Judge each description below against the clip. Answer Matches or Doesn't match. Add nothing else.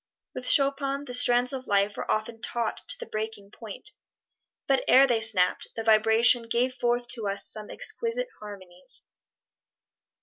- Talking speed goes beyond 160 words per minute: Doesn't match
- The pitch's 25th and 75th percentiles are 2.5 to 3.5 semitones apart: Matches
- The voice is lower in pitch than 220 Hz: Doesn't match